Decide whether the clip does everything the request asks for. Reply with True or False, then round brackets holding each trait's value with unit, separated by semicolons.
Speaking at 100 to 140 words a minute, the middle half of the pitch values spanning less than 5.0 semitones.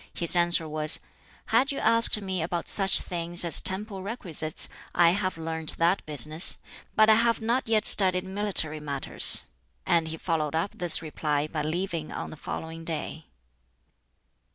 False (155 wpm; 3.7 semitones)